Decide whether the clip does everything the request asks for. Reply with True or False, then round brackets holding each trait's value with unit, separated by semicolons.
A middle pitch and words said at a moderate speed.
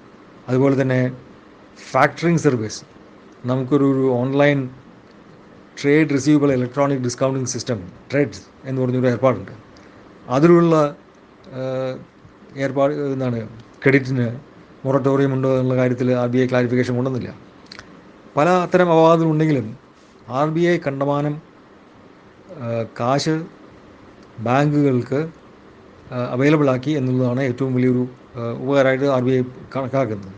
False (130 Hz; 90 wpm)